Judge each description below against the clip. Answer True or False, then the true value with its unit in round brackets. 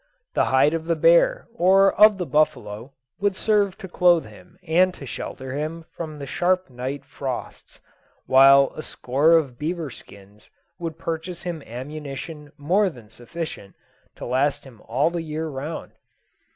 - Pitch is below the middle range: False (155 Hz)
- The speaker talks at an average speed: True (155 wpm)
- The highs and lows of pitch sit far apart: False (4.7 semitones)